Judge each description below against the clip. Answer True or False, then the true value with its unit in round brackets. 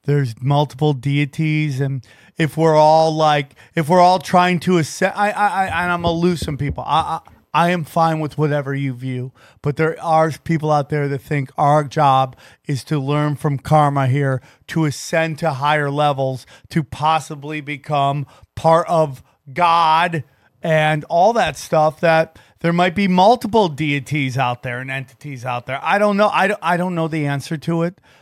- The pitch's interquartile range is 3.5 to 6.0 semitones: False (3.0 semitones)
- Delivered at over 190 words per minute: False (185 wpm)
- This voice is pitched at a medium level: True (150 Hz)